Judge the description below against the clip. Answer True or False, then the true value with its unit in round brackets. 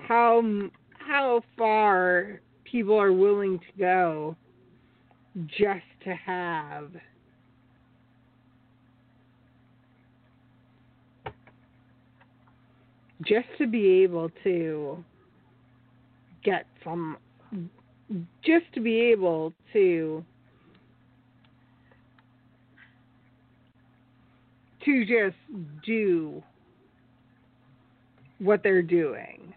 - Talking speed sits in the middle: False (60 wpm)